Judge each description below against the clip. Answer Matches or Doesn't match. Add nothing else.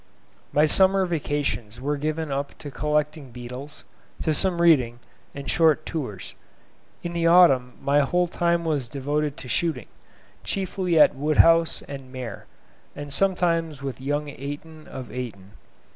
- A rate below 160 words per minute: Matches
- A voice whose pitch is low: Doesn't match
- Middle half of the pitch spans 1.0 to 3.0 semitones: Doesn't match